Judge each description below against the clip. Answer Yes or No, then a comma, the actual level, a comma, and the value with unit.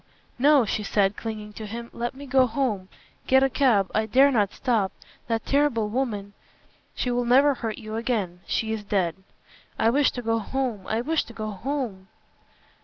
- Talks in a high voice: Yes, high, 230 Hz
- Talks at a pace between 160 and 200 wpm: Yes, average, 185 wpm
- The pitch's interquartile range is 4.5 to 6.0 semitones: No, average, 3.9 semitones